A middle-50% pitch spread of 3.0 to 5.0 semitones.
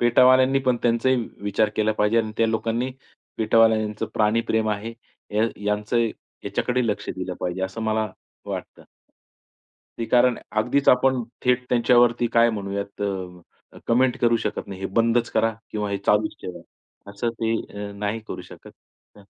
No: narrow, 2.5 semitones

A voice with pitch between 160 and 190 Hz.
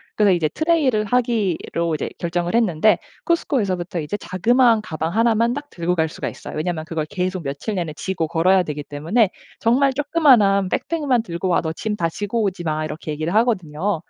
Yes: medium, 185 Hz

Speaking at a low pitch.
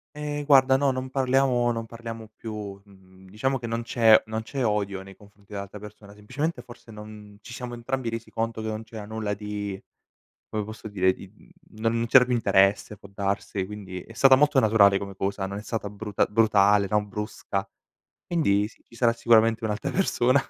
Yes: low, 110 Hz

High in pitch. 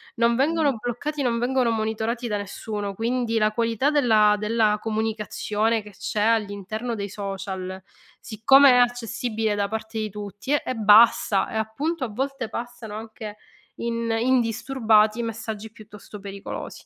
Yes: high, 220 Hz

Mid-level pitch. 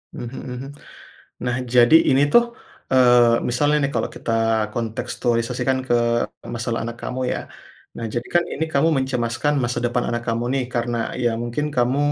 No: low, 120 Hz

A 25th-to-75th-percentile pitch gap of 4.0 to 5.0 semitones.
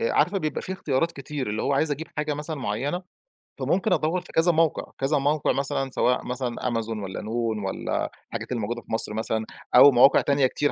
Yes: average, 4.7 semitones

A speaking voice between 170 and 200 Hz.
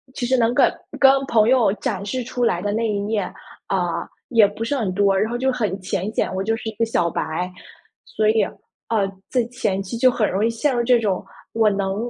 No: high, 220 Hz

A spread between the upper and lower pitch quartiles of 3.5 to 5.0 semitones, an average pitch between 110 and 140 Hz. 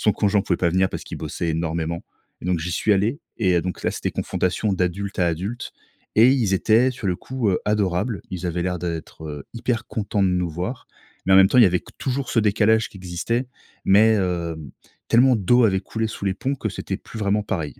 No: average, 3.9 semitones; very low, 95 Hz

